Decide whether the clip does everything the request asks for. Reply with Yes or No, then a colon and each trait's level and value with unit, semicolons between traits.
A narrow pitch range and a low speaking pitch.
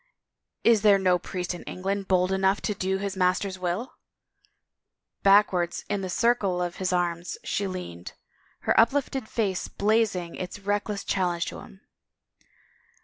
No: narrow, 2.2 semitones; high, 190 Hz